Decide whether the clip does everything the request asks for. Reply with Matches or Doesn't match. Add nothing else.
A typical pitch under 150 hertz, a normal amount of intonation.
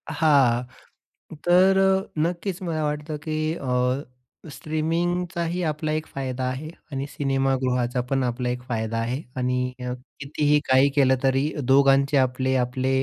Matches